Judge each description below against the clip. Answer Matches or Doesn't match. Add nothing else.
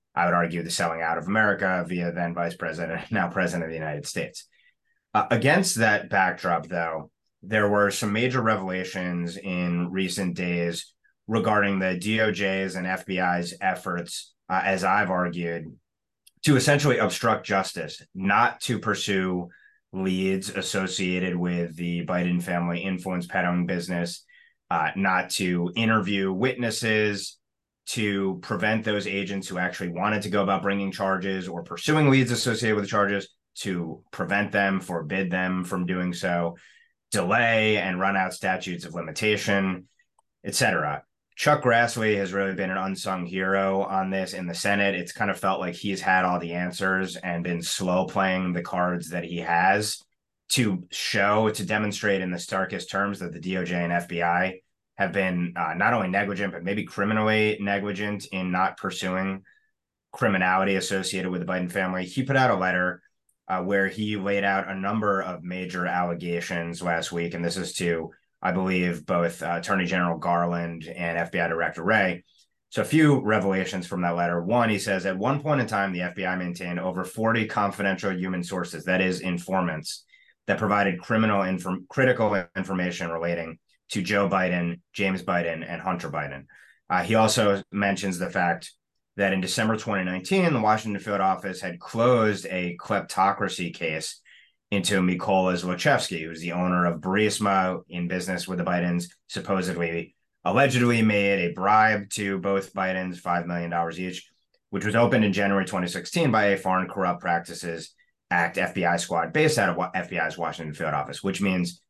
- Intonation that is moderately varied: Doesn't match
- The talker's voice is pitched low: Matches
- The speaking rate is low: Doesn't match